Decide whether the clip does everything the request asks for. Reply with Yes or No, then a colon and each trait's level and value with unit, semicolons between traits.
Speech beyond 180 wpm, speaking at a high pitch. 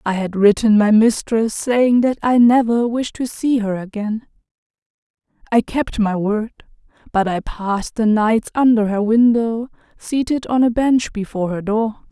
No: average, 165 wpm; high, 225 Hz